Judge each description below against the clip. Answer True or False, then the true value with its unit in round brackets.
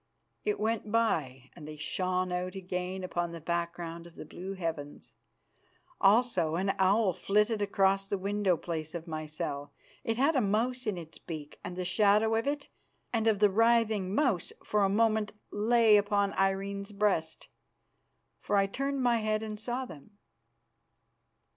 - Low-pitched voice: False (195 Hz)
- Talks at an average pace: True (160 wpm)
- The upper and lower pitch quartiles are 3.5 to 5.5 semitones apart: True (3.9 semitones)